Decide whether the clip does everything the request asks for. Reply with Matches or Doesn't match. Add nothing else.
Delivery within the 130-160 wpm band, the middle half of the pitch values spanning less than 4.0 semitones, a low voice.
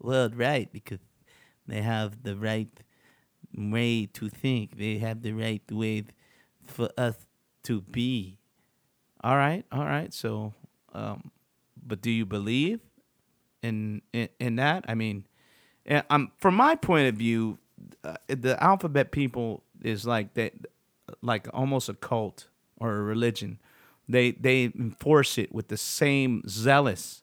Matches